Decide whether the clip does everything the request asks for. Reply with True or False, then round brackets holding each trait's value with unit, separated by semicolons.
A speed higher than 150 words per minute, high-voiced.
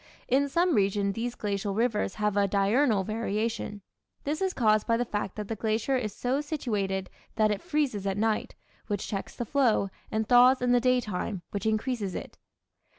True (180 wpm; 220 Hz)